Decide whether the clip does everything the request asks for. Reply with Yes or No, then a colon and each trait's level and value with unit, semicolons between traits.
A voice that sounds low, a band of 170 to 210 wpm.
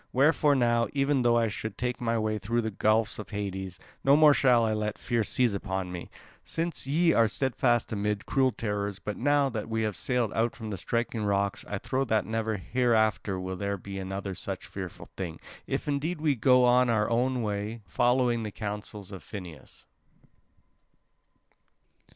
Yes: low, 110 Hz; average, 175 wpm